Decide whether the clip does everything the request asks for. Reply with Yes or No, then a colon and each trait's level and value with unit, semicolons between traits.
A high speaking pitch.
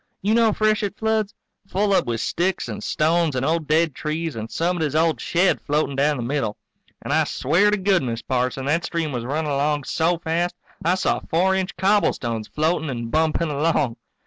No: medium, 160 Hz